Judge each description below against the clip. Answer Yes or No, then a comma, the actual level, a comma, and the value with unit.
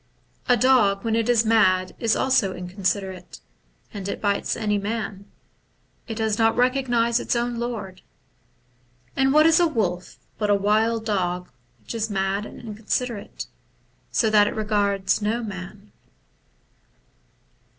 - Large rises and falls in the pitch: No, average, 2.9 semitones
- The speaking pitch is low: No, high, 215 Hz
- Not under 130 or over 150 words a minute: Yes, average, 140 wpm